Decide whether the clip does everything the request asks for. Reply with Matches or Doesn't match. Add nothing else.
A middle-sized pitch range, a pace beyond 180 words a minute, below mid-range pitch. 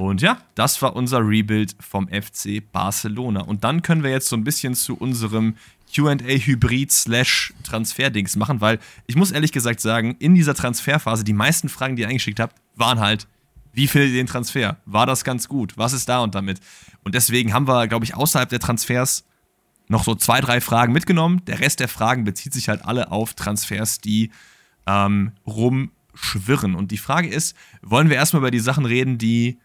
Matches